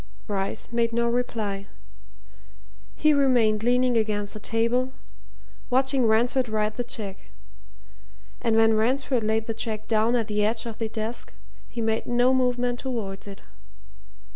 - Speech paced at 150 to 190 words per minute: No, average, 140 wpm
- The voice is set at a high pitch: Yes, high, 230 Hz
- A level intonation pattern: Yes, narrow, 2.3 semitones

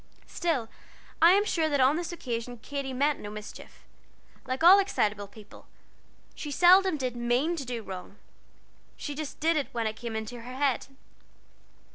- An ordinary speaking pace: Yes, average, 165 wpm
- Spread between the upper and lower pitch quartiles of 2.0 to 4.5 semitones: No, wide, 5.6 semitones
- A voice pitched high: Yes, very high, 265 Hz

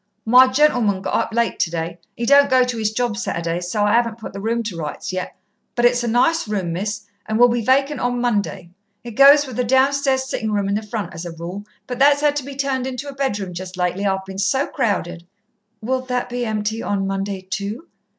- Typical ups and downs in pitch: Yes, average, 4.8 semitones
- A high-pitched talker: Yes, high, 225 Hz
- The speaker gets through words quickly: Yes, fast, 230 wpm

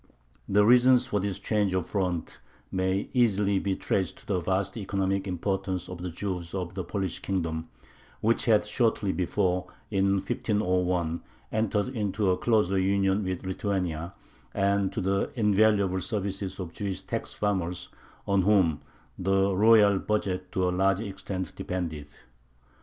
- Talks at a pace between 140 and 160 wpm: Yes, average, 145 wpm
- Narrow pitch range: Yes, narrow, 1.9 semitones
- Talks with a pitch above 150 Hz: No, very low, 95 Hz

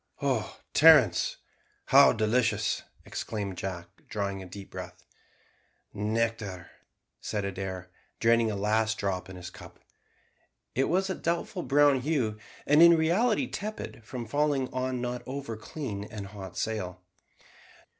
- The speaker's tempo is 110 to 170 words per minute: Yes, slow, 135 wpm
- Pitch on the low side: Yes, low, 110 Hz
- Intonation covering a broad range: Yes, wide, 5.7 semitones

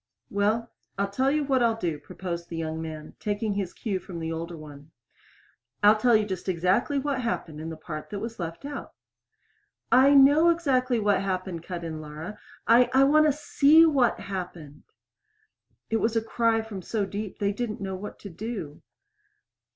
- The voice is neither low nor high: No, high, 205 Hz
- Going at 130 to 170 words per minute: No, average, 185 wpm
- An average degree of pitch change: No, wide, 6.0 semitones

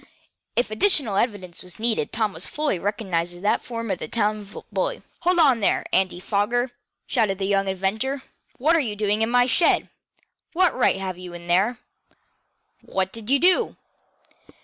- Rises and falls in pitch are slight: No, average, 4.4 semitones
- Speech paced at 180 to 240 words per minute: No, average, 170 wpm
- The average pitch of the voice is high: Yes, high, 215 Hz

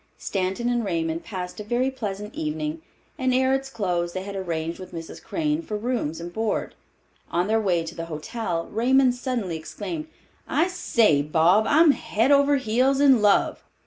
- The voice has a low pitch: No, high, 210 Hz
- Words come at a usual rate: Yes, average, 175 wpm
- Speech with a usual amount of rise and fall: No, wide, 7.0 semitones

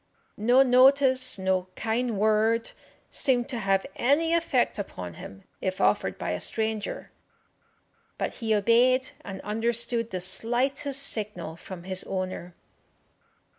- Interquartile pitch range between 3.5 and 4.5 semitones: No, average, 4.9 semitones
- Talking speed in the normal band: No, slow, 125 wpm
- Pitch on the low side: No, high, 225 Hz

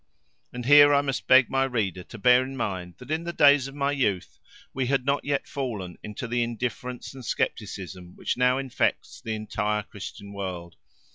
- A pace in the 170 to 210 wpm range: Yes, average, 190 wpm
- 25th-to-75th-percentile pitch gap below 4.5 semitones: No, average, 4.9 semitones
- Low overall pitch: Yes, low, 125 Hz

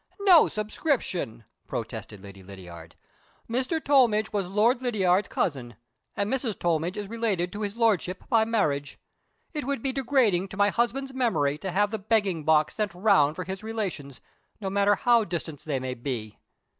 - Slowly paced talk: No, average, 165 wpm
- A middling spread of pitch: No, wide, 6.6 semitones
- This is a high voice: Yes, high, 200 Hz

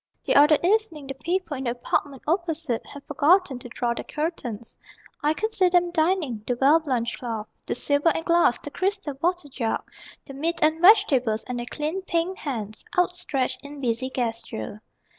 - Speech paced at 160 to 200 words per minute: Yes, average, 180 wpm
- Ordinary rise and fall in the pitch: No, wide, 5.7 semitones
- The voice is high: Yes, very high, 290 Hz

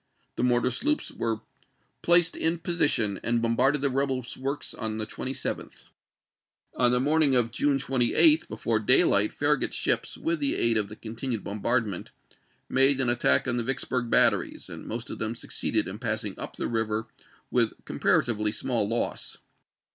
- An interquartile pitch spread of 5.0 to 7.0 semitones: No, average, 3.3 semitones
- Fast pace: No, average, 170 wpm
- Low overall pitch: Yes, low, 120 Hz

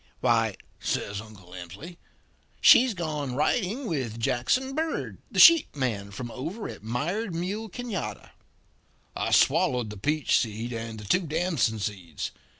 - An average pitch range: No, wide, 8.9 semitones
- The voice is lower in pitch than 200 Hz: Yes, low, 135 Hz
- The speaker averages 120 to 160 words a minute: Yes, average, 140 wpm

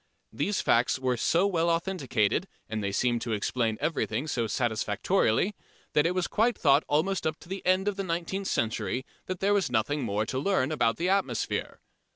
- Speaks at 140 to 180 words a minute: No, average, 190 wpm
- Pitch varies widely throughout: Yes, wide, 8.0 semitones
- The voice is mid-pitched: Yes, medium, 150 Hz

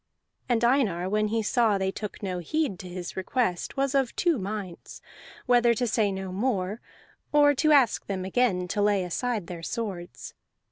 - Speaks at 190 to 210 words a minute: No, average, 175 wpm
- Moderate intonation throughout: Yes, average, 4.9 semitones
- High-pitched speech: Yes, high, 210 Hz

